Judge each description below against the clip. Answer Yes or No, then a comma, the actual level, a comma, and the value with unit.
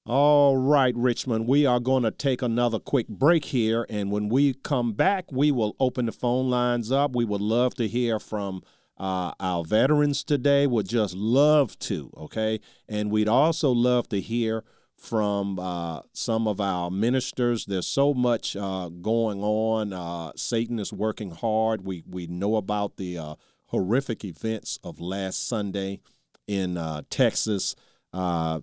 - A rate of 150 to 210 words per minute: Yes, average, 160 wpm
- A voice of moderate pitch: No, low, 110 Hz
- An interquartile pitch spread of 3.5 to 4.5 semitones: Yes, average, 4.1 semitones